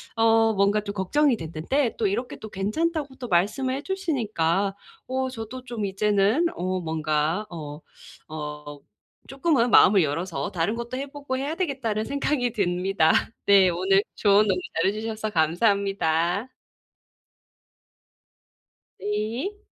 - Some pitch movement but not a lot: No, wide, 6.2 semitones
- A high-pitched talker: Yes, high, 210 Hz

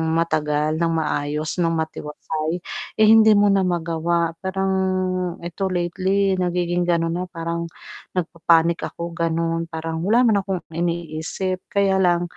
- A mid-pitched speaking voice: Yes, medium, 170 Hz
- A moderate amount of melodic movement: No, narrow, 2.3 semitones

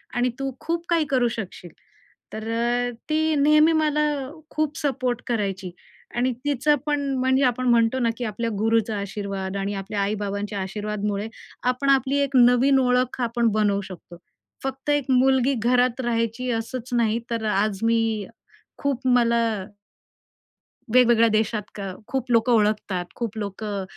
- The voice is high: Yes, high, 235 Hz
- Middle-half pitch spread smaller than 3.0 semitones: No, average, 3.6 semitones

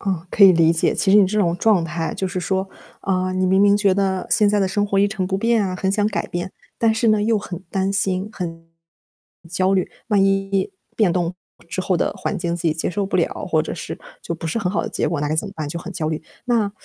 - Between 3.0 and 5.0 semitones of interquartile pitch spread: No, narrow, 2.6 semitones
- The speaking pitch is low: No, high, 190 Hz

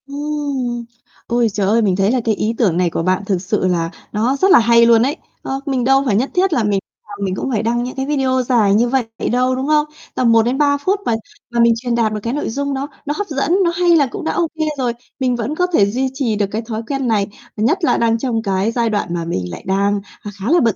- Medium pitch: No, high, 235 Hz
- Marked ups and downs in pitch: No, average, 4.4 semitones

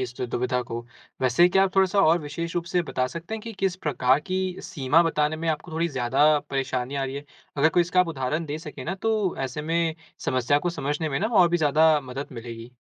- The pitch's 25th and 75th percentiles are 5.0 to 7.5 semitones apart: No, average, 4.6 semitones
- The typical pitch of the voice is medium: Yes, medium, 155 Hz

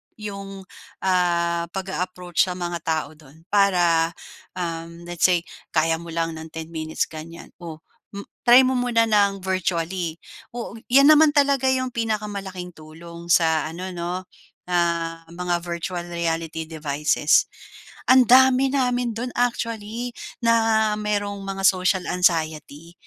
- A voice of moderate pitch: Yes, medium, 180 Hz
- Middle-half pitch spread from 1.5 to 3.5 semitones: No, average, 4.1 semitones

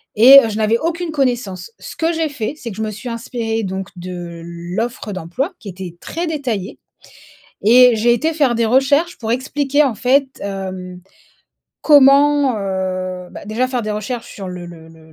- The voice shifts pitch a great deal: Yes, wide, 6.3 semitones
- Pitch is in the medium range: No, high, 225 Hz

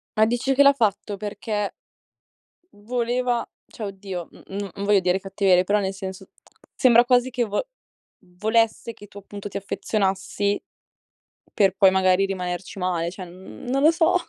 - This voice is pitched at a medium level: No, high, 205 Hz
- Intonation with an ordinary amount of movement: Yes, average, 3.4 semitones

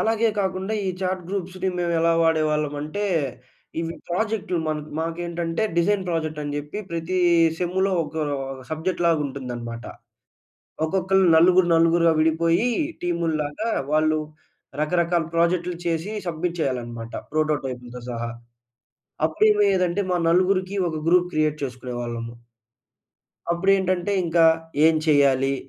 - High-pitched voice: No, medium, 165 Hz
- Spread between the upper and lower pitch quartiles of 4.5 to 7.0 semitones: No, average, 3.2 semitones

